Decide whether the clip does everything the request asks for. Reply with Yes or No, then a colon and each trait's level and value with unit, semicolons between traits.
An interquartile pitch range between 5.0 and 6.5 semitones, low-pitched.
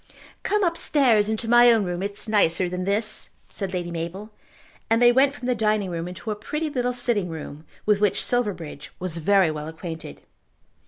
No: wide, 5.5 semitones; high, 205 Hz